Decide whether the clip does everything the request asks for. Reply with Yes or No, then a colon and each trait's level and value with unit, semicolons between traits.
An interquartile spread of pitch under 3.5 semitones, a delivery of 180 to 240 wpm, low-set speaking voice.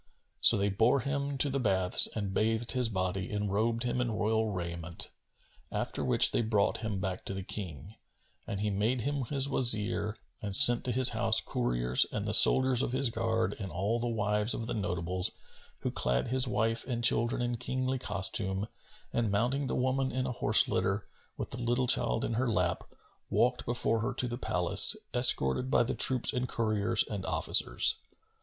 No: average, 3.8 semitones; average, 190 wpm; low, 110 Hz